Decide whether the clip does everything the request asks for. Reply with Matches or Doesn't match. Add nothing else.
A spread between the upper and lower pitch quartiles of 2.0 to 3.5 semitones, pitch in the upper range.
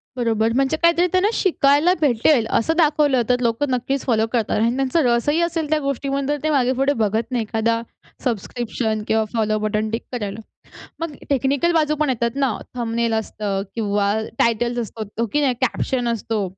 Doesn't match